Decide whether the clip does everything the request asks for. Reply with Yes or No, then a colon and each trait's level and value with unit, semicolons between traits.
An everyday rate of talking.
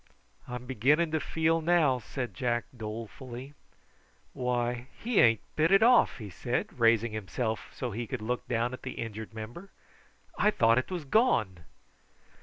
Yes: average, 160 wpm